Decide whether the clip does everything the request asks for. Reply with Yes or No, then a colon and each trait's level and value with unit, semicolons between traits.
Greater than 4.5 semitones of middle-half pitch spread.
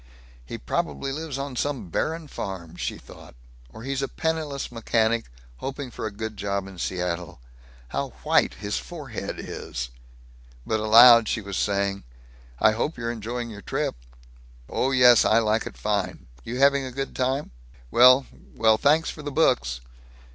Yes: average, 5.3 semitones